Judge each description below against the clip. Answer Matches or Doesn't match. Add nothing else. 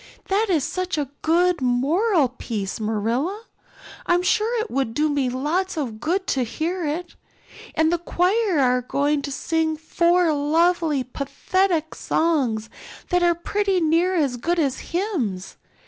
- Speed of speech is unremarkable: Matches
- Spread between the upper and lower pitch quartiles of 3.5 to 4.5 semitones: Doesn't match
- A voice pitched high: Matches